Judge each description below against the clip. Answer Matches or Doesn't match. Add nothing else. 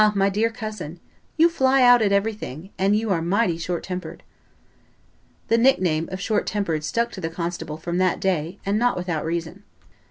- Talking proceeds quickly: Doesn't match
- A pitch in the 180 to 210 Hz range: Matches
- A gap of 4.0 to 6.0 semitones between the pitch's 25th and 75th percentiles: Matches